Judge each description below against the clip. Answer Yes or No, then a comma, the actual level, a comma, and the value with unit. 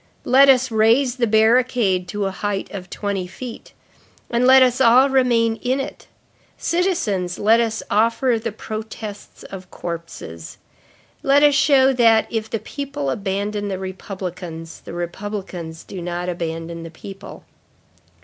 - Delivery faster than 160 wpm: No, average, 140 wpm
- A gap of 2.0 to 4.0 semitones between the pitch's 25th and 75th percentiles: No, average, 5.3 semitones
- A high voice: Yes, high, 215 Hz